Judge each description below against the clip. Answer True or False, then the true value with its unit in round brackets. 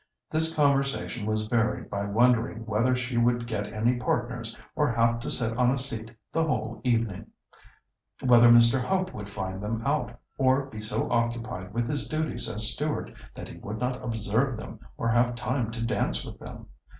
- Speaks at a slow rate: False (180 wpm)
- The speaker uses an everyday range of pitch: False (2.3 semitones)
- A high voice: False (120 Hz)